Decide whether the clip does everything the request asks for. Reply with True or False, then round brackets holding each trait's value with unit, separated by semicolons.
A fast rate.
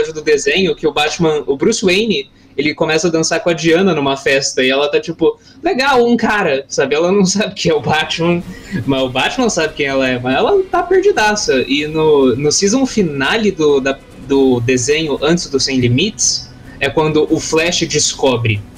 True (190 wpm)